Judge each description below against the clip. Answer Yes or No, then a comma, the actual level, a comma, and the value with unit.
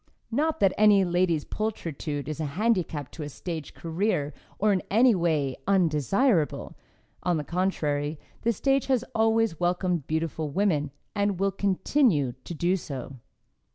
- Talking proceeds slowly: No, average, 145 wpm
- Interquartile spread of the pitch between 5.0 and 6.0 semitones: Yes, average, 5.3 semitones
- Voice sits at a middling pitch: Yes, medium, 175 Hz